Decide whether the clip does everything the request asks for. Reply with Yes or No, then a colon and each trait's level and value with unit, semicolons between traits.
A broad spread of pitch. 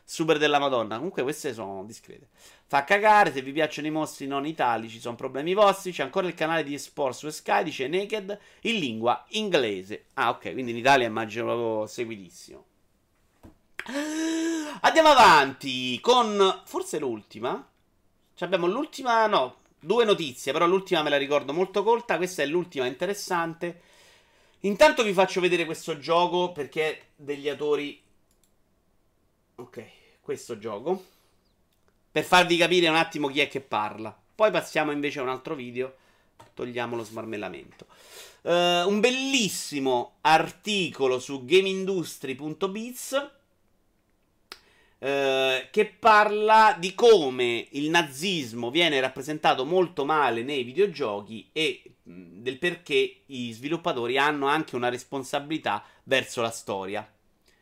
Yes: wide, 7.0 semitones